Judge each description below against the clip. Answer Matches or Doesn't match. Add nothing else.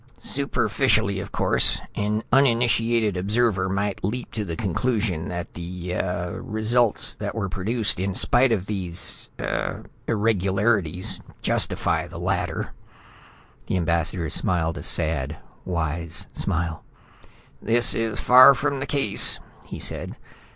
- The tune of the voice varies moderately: Matches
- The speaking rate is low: Matches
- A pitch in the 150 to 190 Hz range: Doesn't match